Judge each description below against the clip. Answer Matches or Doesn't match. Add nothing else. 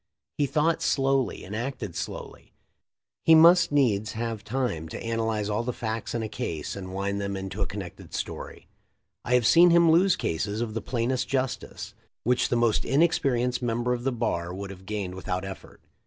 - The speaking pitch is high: Doesn't match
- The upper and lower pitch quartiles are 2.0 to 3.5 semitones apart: Doesn't match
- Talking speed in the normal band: Matches